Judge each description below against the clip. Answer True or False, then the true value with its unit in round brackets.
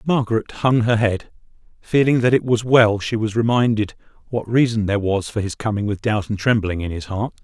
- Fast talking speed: True (210 wpm)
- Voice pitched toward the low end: True (110 Hz)